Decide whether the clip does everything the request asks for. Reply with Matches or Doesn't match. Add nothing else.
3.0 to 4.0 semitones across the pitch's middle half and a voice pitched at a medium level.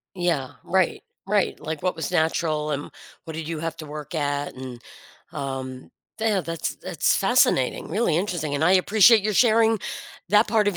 Doesn't match